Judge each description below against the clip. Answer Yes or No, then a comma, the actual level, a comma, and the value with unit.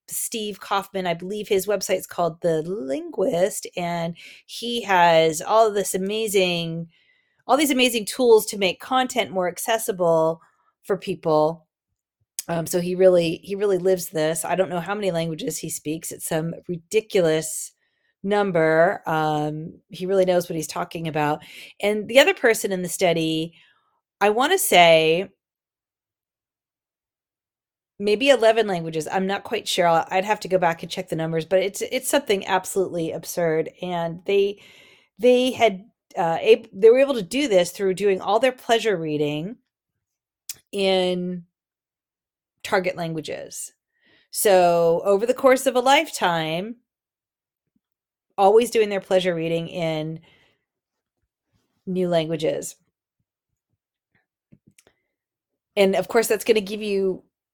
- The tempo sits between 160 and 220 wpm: No, average, 140 wpm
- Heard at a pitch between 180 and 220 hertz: Yes, medium, 185 Hz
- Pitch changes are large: No, average, 4.4 semitones